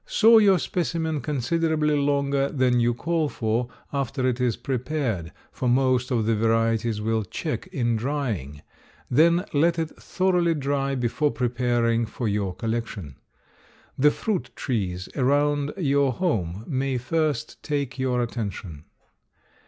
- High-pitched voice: No, low, 130 Hz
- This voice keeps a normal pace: No, slow, 130 wpm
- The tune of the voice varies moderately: Yes, average, 4.4 semitones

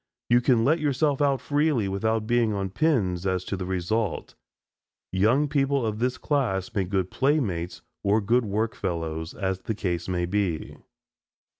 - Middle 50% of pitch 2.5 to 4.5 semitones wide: No, wide, 5.5 semitones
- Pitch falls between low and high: No, low, 105 Hz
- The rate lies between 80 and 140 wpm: No, average, 160 wpm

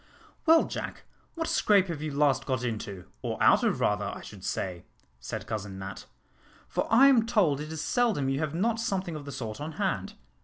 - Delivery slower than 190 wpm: No, average, 200 wpm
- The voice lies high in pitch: No, medium, 150 Hz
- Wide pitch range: Yes, wide, 8.3 semitones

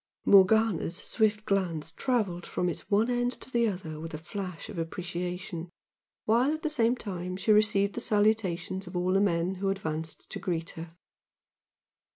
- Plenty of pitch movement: No, average, 3.8 semitones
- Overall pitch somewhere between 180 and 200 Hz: Yes, high, 190 Hz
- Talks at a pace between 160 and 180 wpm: Yes, average, 170 wpm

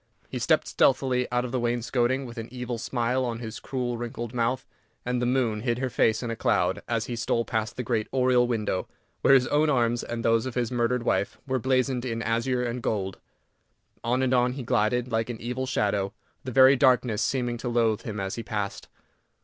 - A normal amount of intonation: No, narrow, 1.7 semitones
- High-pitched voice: No, low, 120 Hz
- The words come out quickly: Yes, fast, 210 wpm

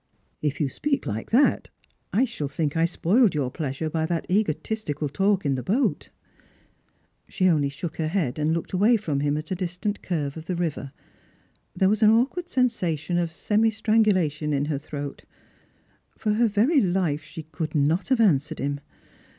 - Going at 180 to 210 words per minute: Yes, average, 185 wpm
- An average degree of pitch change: No, wide, 6.0 semitones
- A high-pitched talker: No, medium, 170 Hz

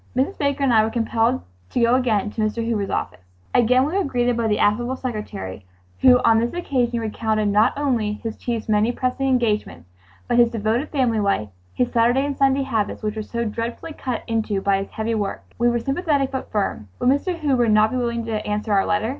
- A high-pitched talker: Yes, high, 230 Hz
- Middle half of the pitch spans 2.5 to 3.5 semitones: Yes, average, 3.2 semitones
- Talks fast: Yes, fast, 210 wpm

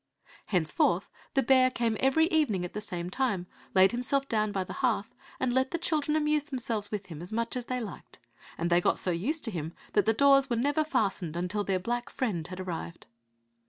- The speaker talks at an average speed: No, fast, 210 wpm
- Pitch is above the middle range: Yes, high, 225 Hz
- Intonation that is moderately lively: No, wide, 6.2 semitones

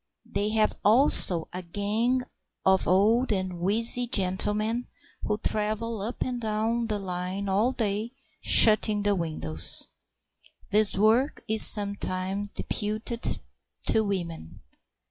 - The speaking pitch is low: No, high, 210 Hz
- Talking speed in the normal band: No, slow, 115 wpm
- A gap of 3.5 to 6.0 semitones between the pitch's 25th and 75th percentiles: No, average, 2.9 semitones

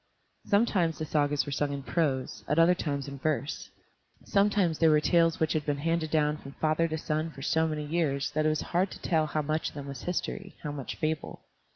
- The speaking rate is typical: No, fast, 225 wpm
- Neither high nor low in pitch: Yes, medium, 155 Hz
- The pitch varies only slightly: Yes, narrow, 2.2 semitones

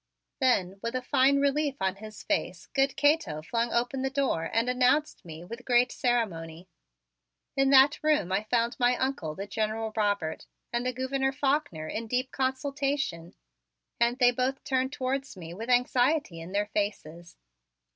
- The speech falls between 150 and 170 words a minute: Yes, average, 160 wpm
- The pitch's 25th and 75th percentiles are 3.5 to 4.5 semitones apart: No, average, 5.1 semitones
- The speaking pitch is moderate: No, high, 245 Hz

